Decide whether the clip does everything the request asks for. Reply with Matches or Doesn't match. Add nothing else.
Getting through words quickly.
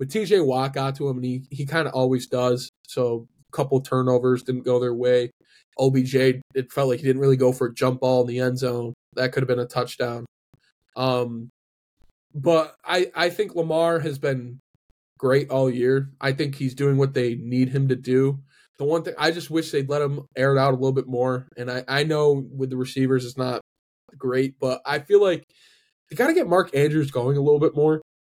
Matches